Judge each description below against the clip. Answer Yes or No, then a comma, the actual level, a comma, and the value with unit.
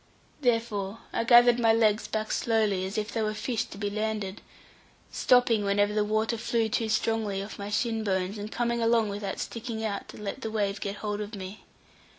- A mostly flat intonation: Yes, narrow, 2.0 semitones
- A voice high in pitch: Yes, high, 215 Hz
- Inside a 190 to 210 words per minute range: Yes, average, 195 wpm